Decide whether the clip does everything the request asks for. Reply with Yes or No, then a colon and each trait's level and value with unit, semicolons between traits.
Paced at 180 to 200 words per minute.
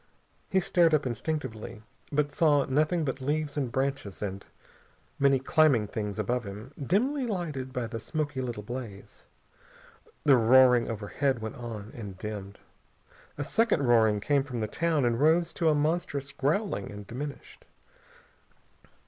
No: average, 145 wpm